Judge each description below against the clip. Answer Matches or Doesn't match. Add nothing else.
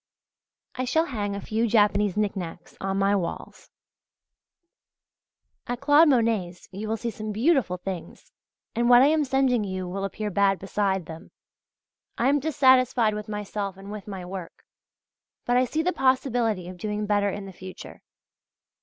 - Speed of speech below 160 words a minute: Doesn't match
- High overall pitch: Matches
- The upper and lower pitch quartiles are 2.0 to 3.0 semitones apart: Doesn't match